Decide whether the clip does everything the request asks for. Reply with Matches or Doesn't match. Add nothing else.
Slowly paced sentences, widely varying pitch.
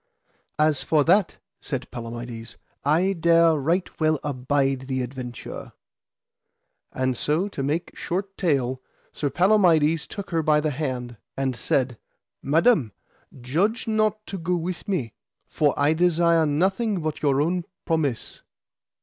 Doesn't match